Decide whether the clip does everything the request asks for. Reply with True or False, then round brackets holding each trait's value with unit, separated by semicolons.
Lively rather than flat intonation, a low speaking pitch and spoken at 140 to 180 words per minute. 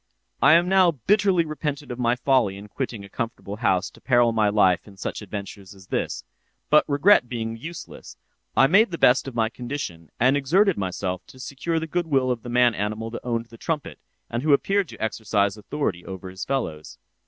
False (6.2 semitones; 120 Hz; 190 wpm)